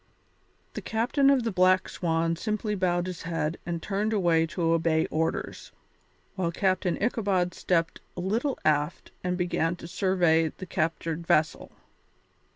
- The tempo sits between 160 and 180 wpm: No, average, 145 wpm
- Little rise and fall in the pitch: No, average, 3.0 semitones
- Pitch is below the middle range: No, medium, 175 Hz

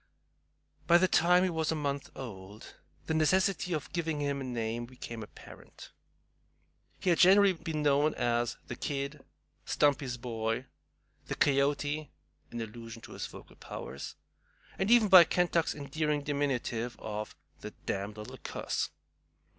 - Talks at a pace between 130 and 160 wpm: Yes, average, 140 wpm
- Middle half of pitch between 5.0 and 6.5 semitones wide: Yes, average, 5.3 semitones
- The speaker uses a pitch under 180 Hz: Yes, medium, 140 Hz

